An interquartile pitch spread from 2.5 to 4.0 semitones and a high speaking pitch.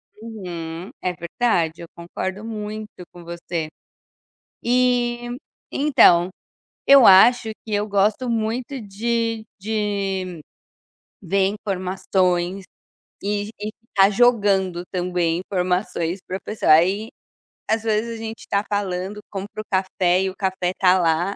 Yes: average, 3.3 semitones; high, 195 Hz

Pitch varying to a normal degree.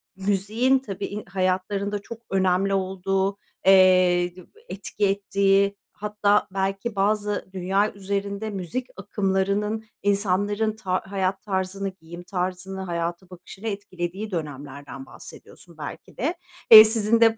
No: narrow, 1.8 semitones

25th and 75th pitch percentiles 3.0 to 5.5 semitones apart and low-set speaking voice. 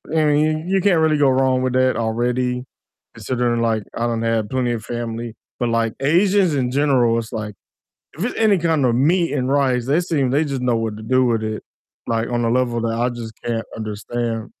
Yes: average, 3.8 semitones; low, 125 Hz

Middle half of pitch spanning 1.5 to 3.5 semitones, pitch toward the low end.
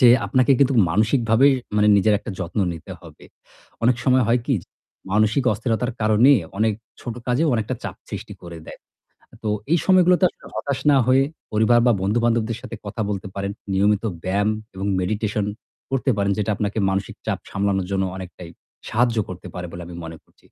No: average, 3.9 semitones; low, 110 Hz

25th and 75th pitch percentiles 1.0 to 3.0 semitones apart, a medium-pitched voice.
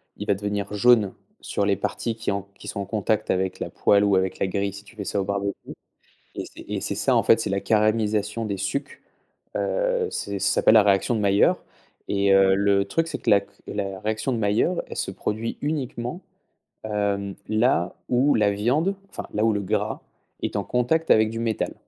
No: narrow, 2.5 semitones; low, 105 Hz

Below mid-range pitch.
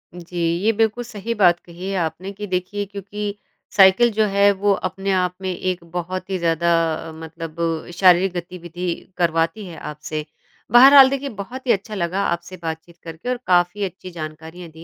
No: medium, 185 Hz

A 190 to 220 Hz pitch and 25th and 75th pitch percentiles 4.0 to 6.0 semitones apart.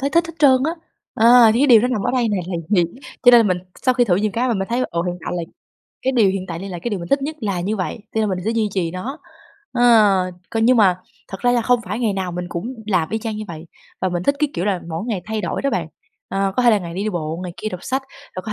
Yes: high, 215 Hz; average, 5.0 semitones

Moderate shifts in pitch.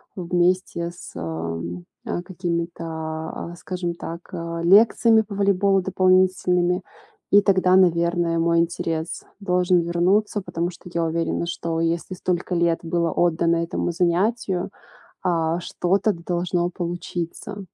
No: narrow, 1.6 semitones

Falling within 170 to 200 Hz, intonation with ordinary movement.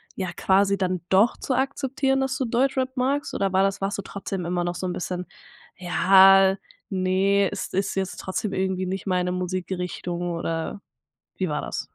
No: high, 190 Hz; narrow, 1.8 semitones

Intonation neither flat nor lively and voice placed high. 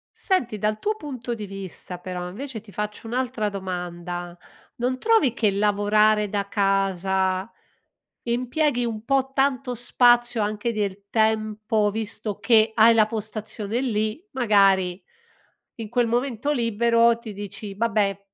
Yes: average, 3.1 semitones; high, 215 Hz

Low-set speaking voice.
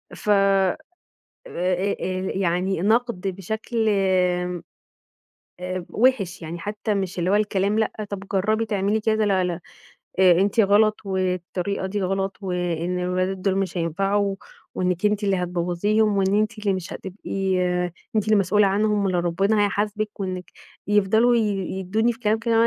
No: high, 195 Hz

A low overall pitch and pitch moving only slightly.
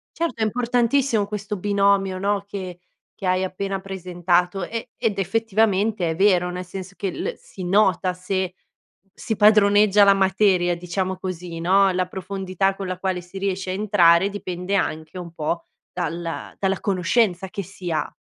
No: high, 190 Hz; narrow, 2.0 semitones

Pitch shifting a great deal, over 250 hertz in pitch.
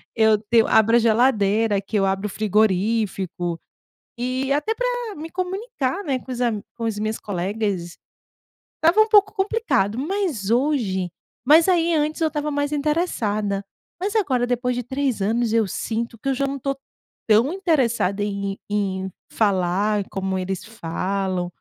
No: wide, 6.5 semitones; high, 230 Hz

